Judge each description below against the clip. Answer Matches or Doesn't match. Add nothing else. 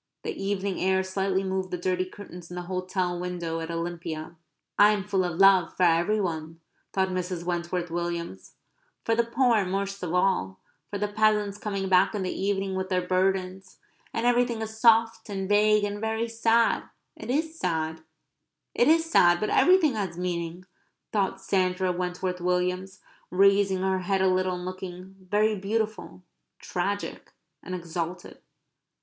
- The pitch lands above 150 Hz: Matches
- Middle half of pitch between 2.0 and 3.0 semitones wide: Matches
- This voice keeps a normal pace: Matches